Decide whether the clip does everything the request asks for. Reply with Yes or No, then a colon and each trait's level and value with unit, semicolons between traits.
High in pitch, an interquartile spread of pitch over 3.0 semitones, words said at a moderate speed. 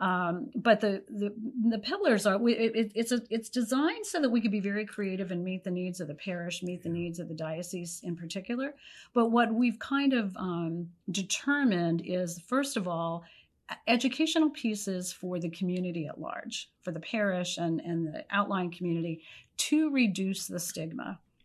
Yes: high, 195 Hz; average, 5.0 semitones; average, 180 wpm